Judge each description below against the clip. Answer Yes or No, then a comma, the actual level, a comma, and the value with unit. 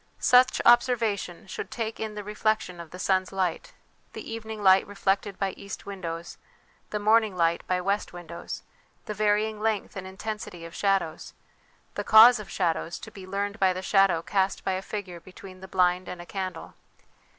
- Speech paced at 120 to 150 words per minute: No, average, 175 wpm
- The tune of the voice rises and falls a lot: No, narrow, 2.5 semitones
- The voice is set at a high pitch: Yes, high, 195 Hz